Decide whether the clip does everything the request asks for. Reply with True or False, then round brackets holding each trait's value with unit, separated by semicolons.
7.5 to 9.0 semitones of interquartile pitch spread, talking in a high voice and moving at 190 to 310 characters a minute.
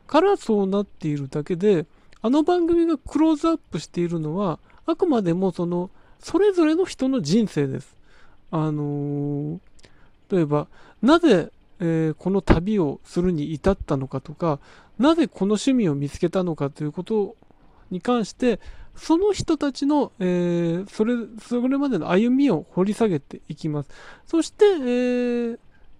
True (8.7 semitones; 195 Hz; 290 characters per minute)